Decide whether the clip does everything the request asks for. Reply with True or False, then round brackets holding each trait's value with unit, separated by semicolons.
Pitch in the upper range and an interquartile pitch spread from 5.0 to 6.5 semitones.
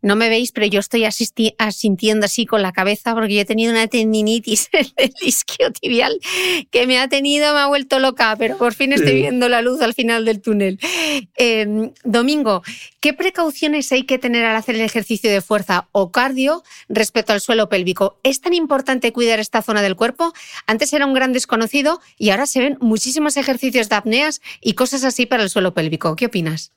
False (235 Hz; 3.8 semitones)